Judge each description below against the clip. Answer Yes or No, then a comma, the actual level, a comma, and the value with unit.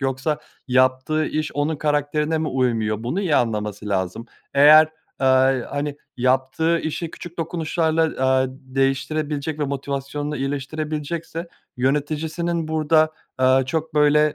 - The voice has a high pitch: No, medium, 145 Hz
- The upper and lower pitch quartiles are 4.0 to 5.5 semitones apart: No, average, 3.0 semitones